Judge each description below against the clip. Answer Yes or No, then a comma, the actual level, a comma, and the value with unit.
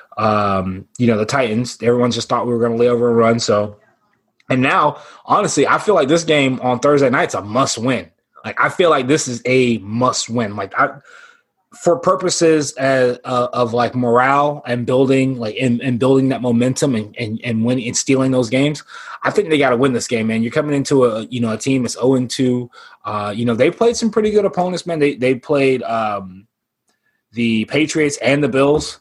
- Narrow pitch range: No, average, 3.4 semitones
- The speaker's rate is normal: No, fast, 215 wpm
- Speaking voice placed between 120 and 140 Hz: Yes, low, 125 Hz